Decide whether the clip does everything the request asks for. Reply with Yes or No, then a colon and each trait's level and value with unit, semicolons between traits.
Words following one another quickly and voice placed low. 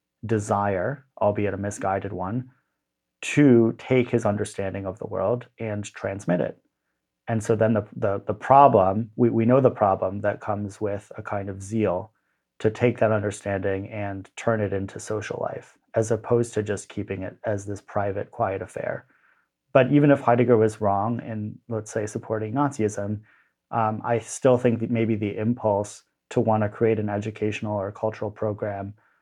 No: average, 170 wpm; low, 105 Hz